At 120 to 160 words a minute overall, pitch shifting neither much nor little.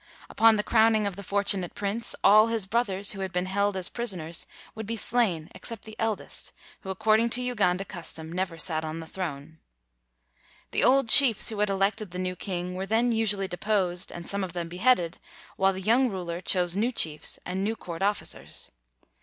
No: average, 195 wpm; average, 3.6 semitones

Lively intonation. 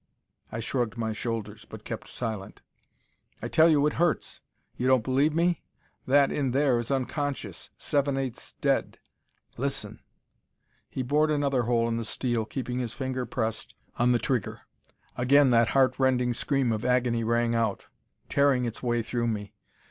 No: average, 3.0 semitones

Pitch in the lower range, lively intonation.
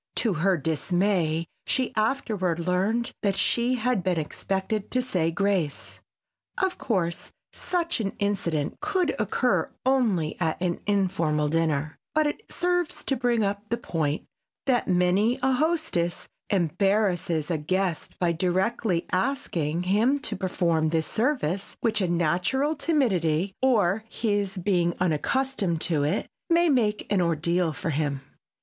No: high, 190 Hz; wide, 5.9 semitones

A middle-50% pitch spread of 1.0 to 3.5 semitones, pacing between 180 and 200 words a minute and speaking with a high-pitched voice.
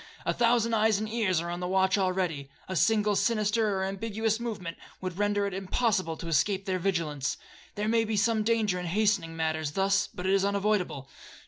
Yes: average, 3.2 semitones; average, 190 wpm; high, 195 Hz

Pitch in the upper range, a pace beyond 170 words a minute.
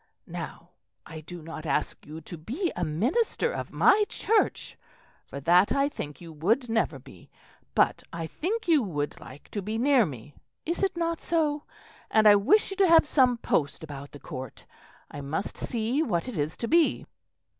Yes: high, 215 Hz; average, 185 wpm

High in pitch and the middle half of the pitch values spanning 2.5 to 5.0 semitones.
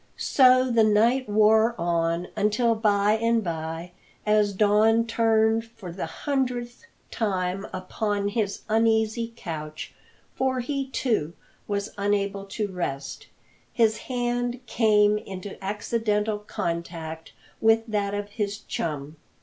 Yes: high, 210 Hz; average, 2.9 semitones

